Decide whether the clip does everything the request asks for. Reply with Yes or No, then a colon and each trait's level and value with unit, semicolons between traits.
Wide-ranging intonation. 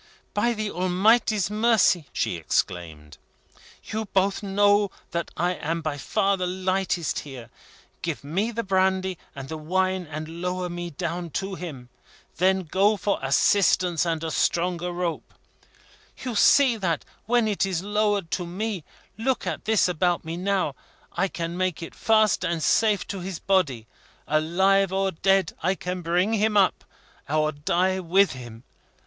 No: average, 3.1 semitones